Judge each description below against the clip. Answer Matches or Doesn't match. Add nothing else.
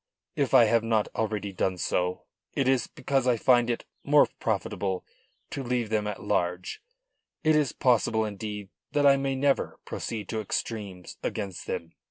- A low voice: Matches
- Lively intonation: Doesn't match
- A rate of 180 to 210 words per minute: Doesn't match